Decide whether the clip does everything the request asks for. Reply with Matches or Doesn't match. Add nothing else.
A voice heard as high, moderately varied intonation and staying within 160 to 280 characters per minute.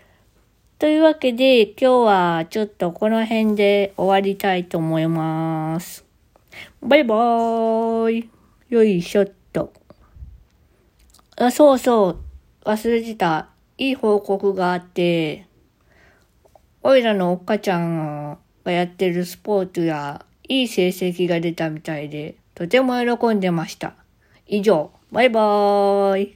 Matches